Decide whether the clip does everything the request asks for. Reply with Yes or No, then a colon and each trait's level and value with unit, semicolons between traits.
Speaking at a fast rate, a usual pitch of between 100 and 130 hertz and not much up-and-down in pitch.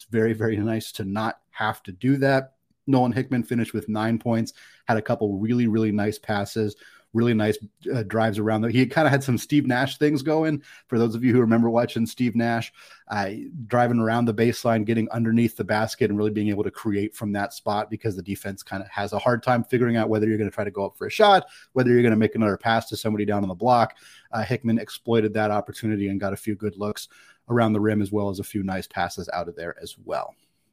Yes: fast, 245 wpm; low, 110 Hz; narrow, 2.2 semitones